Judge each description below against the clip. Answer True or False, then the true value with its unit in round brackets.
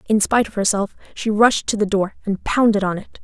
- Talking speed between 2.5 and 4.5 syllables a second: False (5.7 syllables/s)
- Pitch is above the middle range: True (210 Hz)